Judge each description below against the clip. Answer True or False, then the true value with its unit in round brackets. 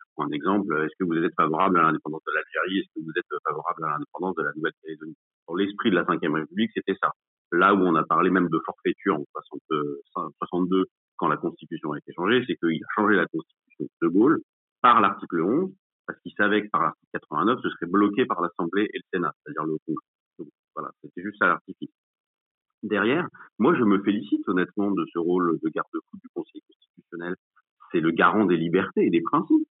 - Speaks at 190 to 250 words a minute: True (205 wpm)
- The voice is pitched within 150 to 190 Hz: True (185 Hz)